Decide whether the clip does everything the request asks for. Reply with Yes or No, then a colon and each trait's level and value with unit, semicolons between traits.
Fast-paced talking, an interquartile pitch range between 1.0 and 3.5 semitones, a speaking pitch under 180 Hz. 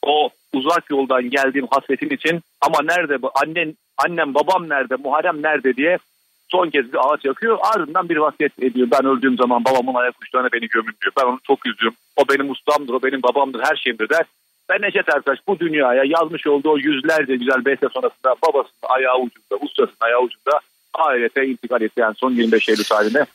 Yes: fast, 185 wpm; average, 3.0 semitones; low, 135 Hz